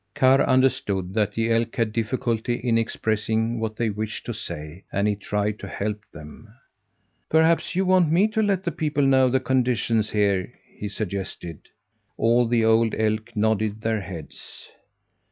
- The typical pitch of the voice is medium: No, low, 110 Hz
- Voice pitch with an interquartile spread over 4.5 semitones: No, average, 3.6 semitones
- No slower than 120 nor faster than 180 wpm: Yes, average, 160 wpm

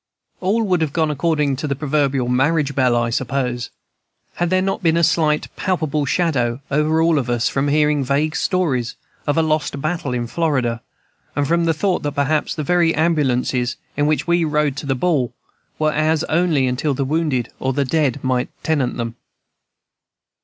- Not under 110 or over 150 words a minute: No, average, 180 wpm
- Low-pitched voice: No, medium, 150 Hz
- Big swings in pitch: No, average, 3.5 semitones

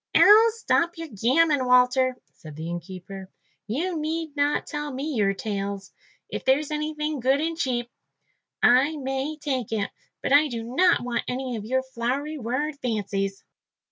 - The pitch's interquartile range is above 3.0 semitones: Yes, average, 5.0 semitones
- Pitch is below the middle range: No, very high, 260 Hz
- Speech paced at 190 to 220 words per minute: No, average, 155 wpm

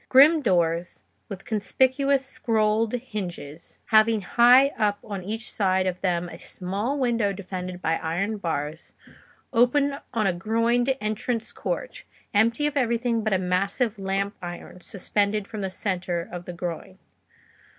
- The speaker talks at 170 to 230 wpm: No, average, 140 wpm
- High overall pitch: Yes, high, 210 Hz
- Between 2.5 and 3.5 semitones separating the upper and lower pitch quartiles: No, average, 4.4 semitones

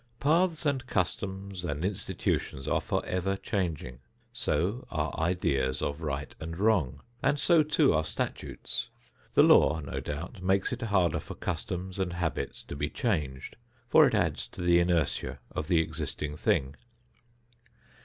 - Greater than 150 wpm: No, average, 145 wpm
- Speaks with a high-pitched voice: No, very low, 90 Hz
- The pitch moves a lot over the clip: No, average, 4.9 semitones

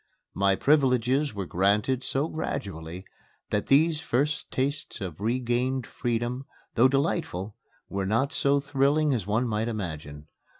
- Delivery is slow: Yes, slow, 130 wpm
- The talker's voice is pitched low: Yes, low, 120 Hz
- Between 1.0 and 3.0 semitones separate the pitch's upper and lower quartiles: No, wide, 5.5 semitones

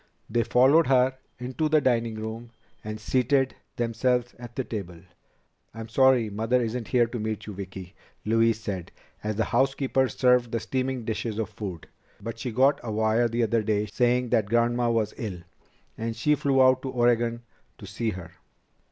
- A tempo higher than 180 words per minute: No, average, 175 wpm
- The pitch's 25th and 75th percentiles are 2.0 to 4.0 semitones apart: Yes, narrow, 2.6 semitones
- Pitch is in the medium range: No, low, 115 Hz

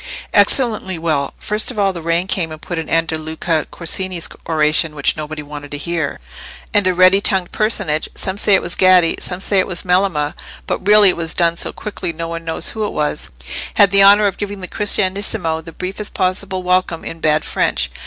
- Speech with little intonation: No, average, 3.4 semitones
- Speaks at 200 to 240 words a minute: Yes, fast, 205 wpm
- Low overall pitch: No, medium, 180 Hz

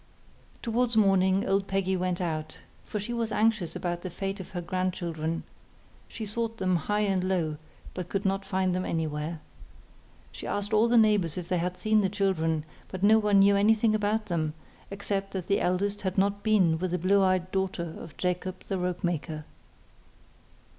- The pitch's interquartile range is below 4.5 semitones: Yes, narrow, 2.6 semitones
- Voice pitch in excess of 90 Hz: Yes, high, 190 Hz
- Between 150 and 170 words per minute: No, average, 180 wpm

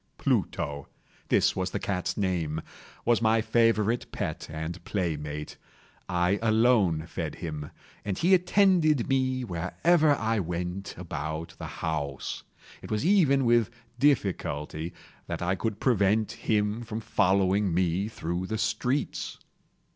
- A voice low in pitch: Yes, low, 100 Hz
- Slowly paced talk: Yes, slow, 120 wpm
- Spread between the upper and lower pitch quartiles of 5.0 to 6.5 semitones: Yes, wide, 5.4 semitones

